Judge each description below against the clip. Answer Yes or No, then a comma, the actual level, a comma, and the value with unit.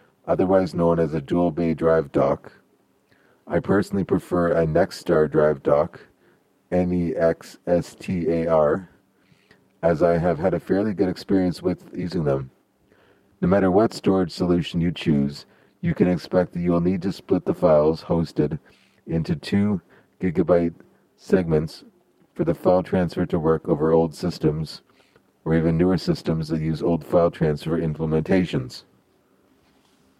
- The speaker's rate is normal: Yes, average, 150 wpm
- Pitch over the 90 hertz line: No, very low, 85 Hz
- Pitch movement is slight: Yes, narrow, 1.8 semitones